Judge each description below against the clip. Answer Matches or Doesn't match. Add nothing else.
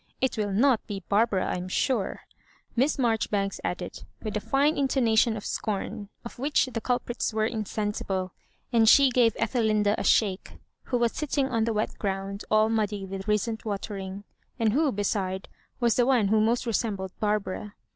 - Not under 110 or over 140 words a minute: Doesn't match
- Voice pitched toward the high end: Matches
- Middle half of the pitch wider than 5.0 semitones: Doesn't match